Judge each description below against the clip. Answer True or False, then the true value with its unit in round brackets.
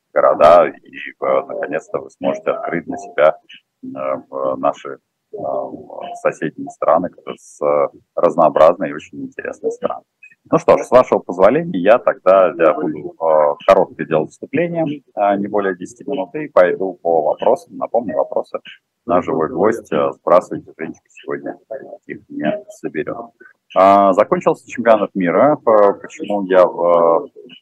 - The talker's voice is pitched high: False (105 Hz)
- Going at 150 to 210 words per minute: False (125 wpm)